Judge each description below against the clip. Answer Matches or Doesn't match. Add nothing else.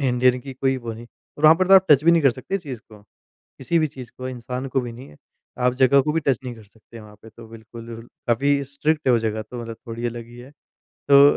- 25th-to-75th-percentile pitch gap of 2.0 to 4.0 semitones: Matches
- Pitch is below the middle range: Matches